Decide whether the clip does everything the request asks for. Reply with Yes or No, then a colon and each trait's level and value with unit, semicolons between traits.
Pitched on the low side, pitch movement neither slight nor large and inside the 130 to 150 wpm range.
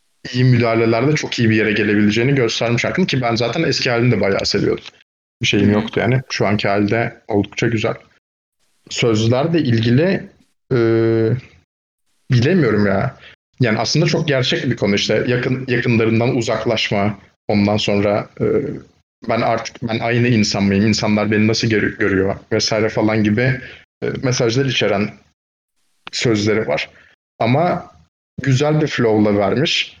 Yes: low, 115 Hz; average, 3.0 semitones; average, 135 wpm